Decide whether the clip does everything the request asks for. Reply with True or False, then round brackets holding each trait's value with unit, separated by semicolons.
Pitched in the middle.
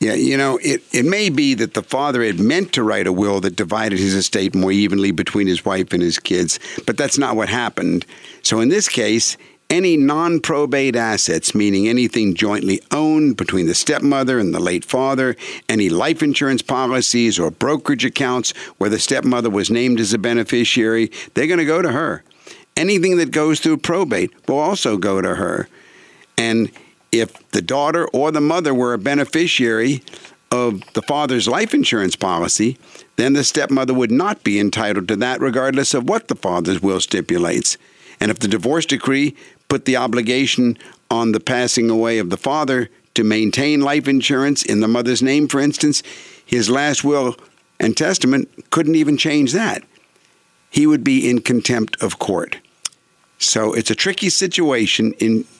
False (125 Hz)